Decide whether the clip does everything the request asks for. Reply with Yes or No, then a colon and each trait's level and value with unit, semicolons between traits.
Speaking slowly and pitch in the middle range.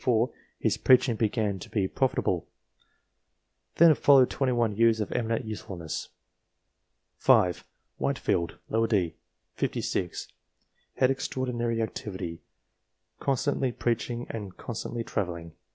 No: slow, 120 wpm; low, 115 Hz